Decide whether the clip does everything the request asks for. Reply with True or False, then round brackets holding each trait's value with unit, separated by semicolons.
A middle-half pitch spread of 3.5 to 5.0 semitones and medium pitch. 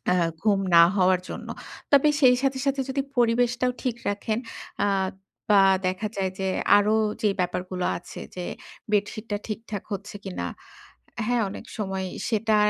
False (3.9 semitones; 210 Hz)